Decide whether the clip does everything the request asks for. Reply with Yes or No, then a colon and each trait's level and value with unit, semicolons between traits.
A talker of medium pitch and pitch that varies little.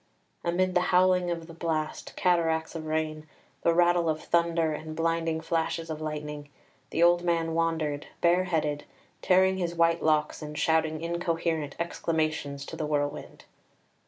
Yes: medium, 165 Hz; narrow, 1.6 semitones